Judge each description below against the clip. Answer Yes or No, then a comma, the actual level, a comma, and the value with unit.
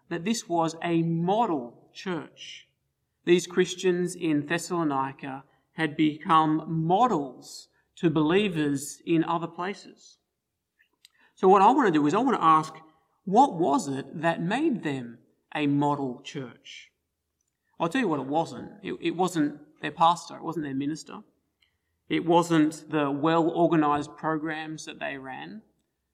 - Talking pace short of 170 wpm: Yes, average, 140 wpm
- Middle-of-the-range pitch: Yes, medium, 160 Hz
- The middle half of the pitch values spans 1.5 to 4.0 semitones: Yes, average, 2.7 semitones